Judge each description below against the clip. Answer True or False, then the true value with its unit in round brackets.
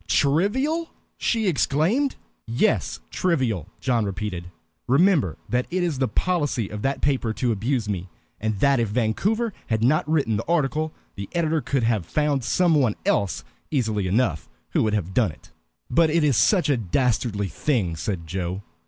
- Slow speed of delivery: False (165 wpm)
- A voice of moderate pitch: False (125 Hz)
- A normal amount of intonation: False (6.9 semitones)